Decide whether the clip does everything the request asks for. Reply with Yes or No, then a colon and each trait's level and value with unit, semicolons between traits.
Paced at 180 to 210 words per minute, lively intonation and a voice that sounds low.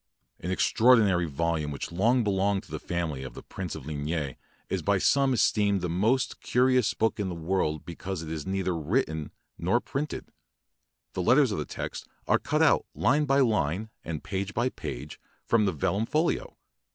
Yes: average, 185 wpm; wide, 6.2 semitones; very low, 95 Hz